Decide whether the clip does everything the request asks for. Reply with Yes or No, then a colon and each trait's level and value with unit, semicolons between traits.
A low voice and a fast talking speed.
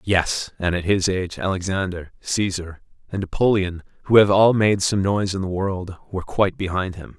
No: very low, 95 Hz; average, 185 wpm